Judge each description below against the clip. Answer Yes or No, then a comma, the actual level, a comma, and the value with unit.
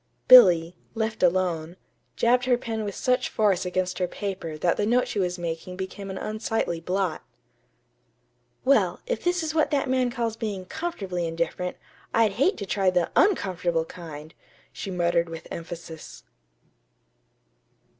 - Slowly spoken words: No, average, 145 wpm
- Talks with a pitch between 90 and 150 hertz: No, high, 190 Hz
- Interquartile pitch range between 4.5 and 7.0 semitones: Yes, average, 4.9 semitones